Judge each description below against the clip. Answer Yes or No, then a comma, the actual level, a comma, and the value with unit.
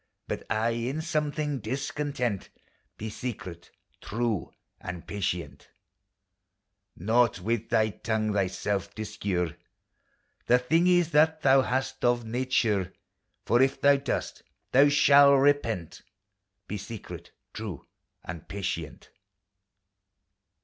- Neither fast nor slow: No, slow, 105 wpm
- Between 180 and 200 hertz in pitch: No, low, 115 Hz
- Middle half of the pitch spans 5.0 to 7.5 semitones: Yes, wide, 5.4 semitones